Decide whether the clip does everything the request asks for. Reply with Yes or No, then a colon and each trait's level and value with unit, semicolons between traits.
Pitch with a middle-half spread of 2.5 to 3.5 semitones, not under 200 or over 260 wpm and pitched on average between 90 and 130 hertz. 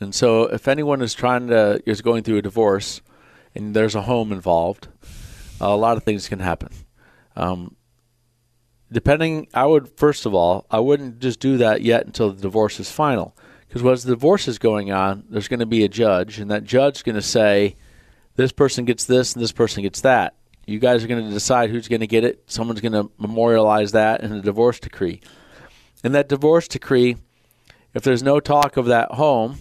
Yes: average, 3.1 semitones; fast, 205 wpm; low, 115 Hz